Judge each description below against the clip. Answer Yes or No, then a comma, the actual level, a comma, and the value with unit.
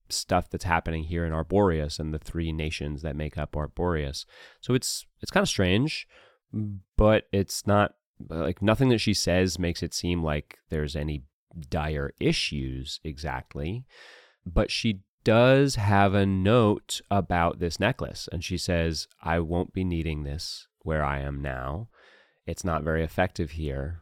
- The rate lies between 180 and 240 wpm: No, average, 155 wpm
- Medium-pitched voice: No, very low, 85 Hz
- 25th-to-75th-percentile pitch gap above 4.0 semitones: Yes, average, 4.5 semitones